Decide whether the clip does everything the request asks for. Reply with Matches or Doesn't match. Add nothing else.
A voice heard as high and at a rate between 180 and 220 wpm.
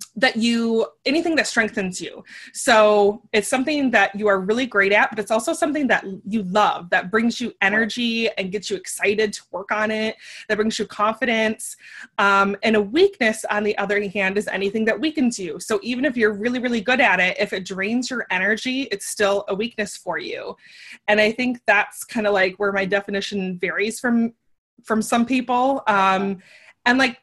Matches